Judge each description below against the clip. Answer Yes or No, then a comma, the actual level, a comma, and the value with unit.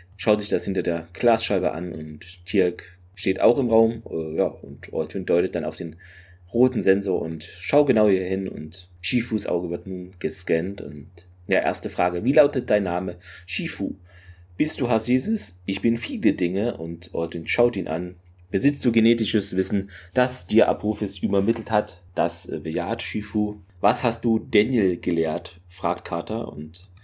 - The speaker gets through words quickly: No, average, 165 wpm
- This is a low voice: Yes, very low, 95 Hz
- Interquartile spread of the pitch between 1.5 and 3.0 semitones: No, average, 4.1 semitones